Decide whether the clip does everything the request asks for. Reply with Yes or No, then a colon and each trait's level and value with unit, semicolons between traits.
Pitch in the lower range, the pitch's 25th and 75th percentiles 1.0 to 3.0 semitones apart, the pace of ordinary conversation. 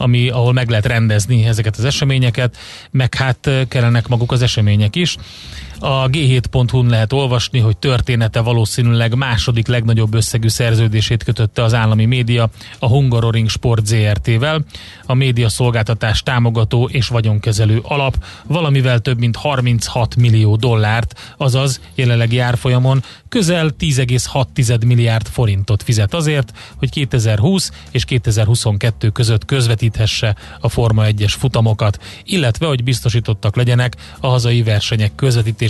Yes: low, 120 Hz; narrow, 2.4 semitones; average, 125 wpm